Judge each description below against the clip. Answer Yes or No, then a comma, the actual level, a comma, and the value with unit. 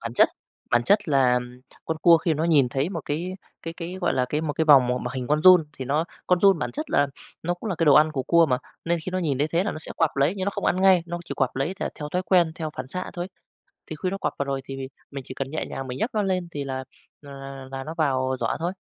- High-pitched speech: No, medium, 155 Hz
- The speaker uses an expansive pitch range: No, average, 4.5 semitones